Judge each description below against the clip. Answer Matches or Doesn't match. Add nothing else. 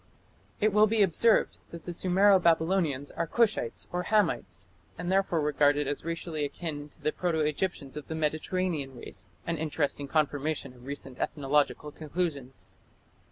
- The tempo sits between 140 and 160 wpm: Matches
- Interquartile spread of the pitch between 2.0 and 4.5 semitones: Matches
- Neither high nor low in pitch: Matches